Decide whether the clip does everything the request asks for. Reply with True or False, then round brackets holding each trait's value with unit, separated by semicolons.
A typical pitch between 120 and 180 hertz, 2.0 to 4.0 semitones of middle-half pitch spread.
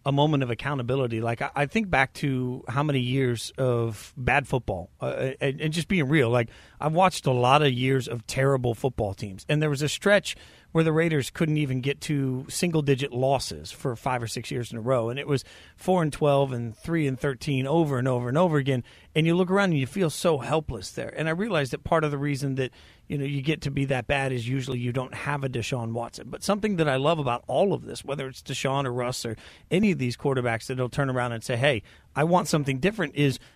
True (135 Hz; 3.3 semitones)